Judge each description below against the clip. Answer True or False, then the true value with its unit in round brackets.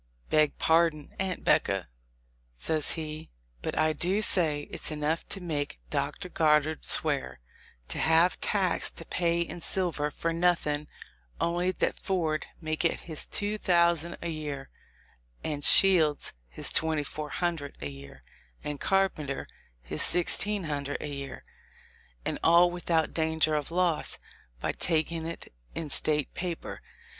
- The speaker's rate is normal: True (145 wpm)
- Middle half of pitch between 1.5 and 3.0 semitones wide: True (2.6 semitones)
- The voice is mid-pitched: True (160 Hz)